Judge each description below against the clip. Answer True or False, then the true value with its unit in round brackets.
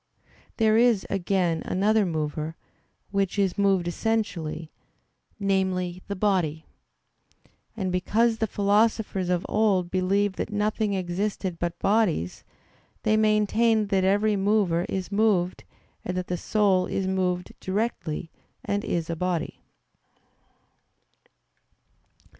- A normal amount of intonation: True (3.0 semitones)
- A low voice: False (195 Hz)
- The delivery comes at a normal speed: False (115 wpm)